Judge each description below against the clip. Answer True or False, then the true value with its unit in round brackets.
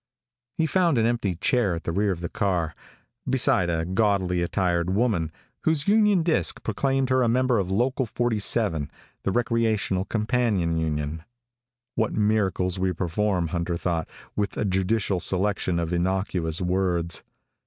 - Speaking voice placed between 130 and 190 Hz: False (95 Hz)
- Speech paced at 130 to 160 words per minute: True (145 wpm)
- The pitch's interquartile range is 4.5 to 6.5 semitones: True (5.0 semitones)